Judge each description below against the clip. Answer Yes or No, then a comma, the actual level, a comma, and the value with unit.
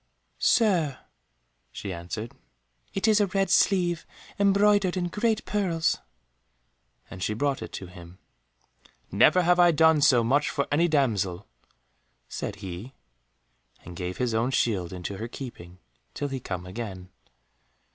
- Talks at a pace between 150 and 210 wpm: No, slow, 135 wpm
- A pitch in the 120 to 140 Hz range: Yes, low, 135 Hz